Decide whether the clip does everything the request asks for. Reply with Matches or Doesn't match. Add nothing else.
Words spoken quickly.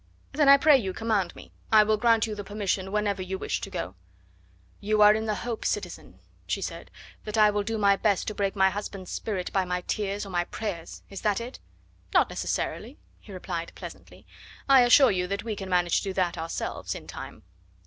Matches